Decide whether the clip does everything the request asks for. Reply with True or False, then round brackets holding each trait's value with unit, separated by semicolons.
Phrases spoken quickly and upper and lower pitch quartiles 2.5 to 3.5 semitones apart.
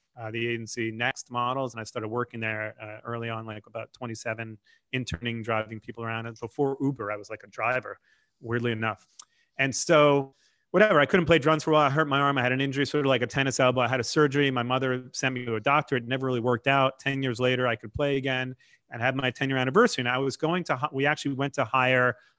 True (250 wpm; 3.0 semitones)